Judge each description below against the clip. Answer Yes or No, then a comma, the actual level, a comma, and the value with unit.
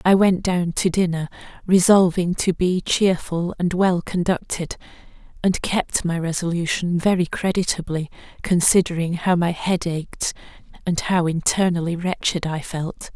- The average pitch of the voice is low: No, medium, 175 Hz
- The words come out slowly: Yes, slow, 130 wpm